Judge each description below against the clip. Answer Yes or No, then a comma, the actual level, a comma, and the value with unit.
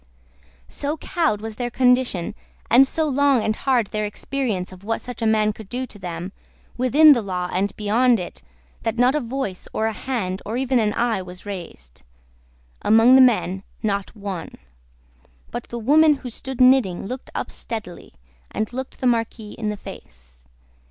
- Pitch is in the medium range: No, high, 225 Hz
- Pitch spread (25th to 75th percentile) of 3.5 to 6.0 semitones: Yes, average, 4.4 semitones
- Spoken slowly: No, average, 175 wpm